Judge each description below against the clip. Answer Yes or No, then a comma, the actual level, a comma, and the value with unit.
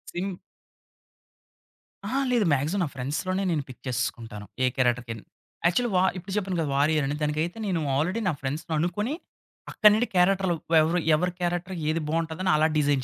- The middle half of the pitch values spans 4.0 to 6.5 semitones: Yes, average, 4.4 semitones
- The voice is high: No, medium, 165 Hz